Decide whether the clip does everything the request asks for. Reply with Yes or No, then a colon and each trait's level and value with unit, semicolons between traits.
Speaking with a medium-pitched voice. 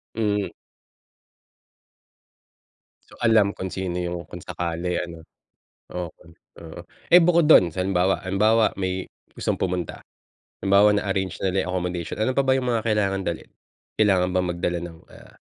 No: very low, 95 Hz